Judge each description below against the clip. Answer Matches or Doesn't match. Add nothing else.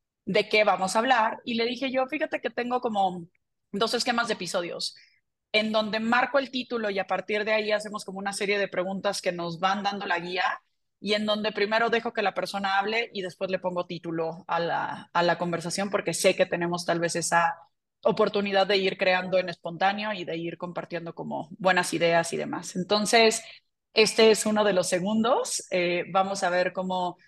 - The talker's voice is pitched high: Matches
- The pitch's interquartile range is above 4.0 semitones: Doesn't match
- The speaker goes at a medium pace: Doesn't match